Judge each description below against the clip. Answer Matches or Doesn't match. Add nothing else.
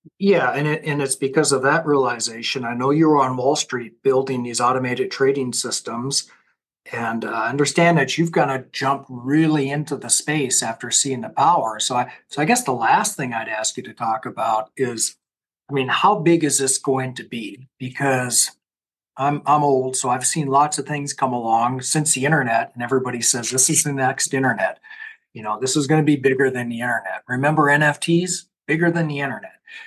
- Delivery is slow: Doesn't match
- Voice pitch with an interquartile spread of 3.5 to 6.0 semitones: Doesn't match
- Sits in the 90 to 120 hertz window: Doesn't match